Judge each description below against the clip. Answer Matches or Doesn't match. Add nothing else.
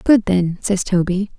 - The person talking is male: Doesn't match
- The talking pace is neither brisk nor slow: Matches